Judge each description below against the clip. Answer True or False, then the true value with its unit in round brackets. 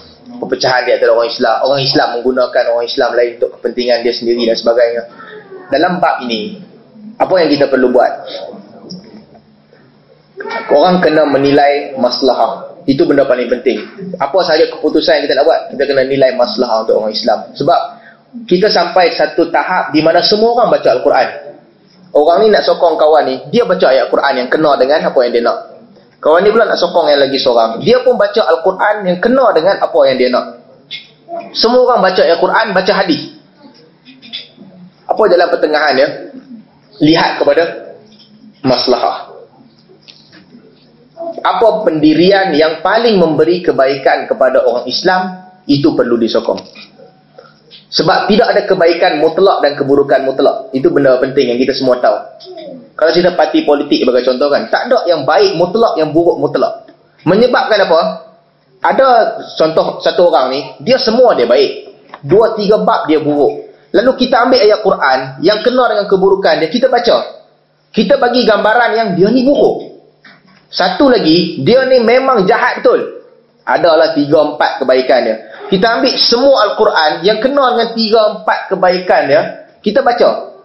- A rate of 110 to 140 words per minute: False (155 wpm)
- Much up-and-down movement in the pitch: True (7.7 semitones)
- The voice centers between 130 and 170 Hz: False (190 Hz)